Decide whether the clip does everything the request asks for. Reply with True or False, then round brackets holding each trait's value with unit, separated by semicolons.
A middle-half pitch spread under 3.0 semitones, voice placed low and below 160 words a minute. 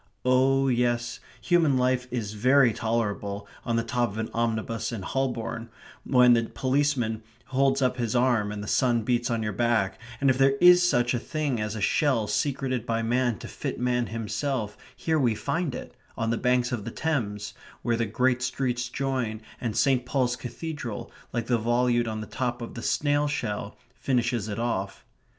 False (2.4 semitones; 120 Hz; 185 wpm)